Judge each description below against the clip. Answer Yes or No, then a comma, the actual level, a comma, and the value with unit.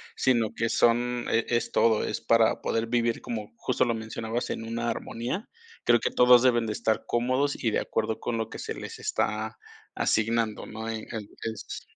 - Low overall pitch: Yes, low, 115 Hz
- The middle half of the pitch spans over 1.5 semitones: No, narrow, 1.2 semitones